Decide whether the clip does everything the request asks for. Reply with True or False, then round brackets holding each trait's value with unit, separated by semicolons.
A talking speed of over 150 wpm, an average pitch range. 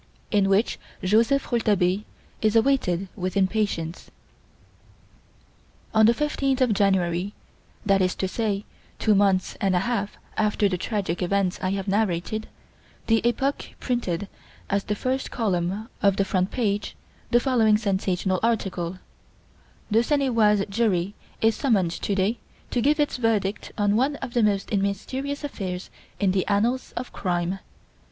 False (145 wpm; 3.4 semitones)